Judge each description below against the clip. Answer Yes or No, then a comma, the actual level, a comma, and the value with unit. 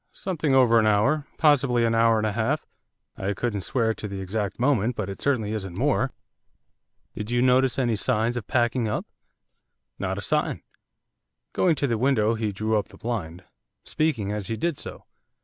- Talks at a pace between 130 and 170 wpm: No, average, 185 wpm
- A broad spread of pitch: No, average, 3.5 semitones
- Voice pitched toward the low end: Yes, low, 115 Hz